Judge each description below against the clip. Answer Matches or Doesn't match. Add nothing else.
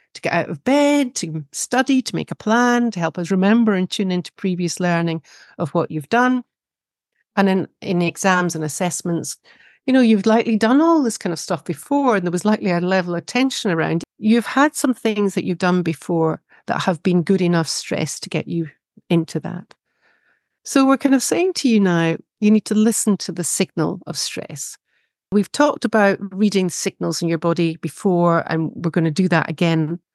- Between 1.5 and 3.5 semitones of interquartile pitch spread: Doesn't match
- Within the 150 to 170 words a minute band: Doesn't match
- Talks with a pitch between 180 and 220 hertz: Matches